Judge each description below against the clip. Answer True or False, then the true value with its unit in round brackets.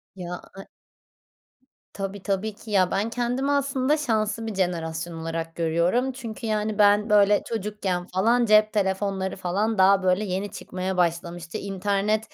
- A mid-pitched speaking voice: False (200 Hz)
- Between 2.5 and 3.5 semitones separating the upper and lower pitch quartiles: True (3.0 semitones)